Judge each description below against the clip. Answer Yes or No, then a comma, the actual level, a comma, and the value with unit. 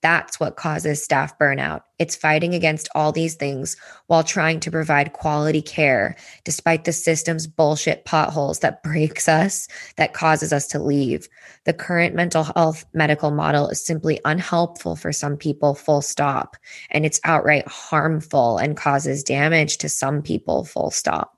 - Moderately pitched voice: Yes, medium, 155 Hz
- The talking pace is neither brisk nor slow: Yes, average, 155 wpm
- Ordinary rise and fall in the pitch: No, narrow, 1.7 semitones